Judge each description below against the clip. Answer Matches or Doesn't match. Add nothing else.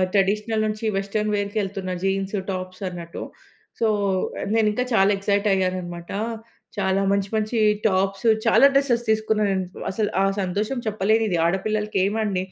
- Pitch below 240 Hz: Matches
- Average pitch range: Doesn't match